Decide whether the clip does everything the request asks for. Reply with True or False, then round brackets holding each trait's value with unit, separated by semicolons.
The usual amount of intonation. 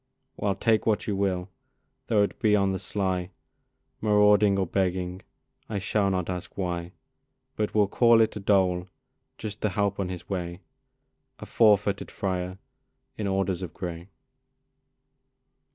False (2.2 semitones)